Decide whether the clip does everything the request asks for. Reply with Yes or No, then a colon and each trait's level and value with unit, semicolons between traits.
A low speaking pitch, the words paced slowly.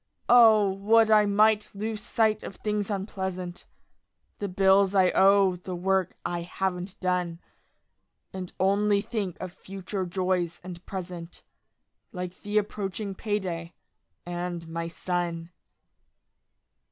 No: high, 190 Hz; slow, 115 wpm